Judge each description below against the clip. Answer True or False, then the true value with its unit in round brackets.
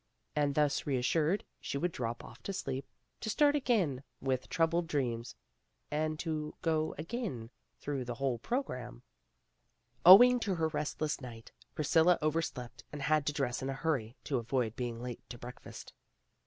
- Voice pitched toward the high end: False (150 Hz)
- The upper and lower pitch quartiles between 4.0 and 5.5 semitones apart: True (4.6 semitones)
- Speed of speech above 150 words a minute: True (160 wpm)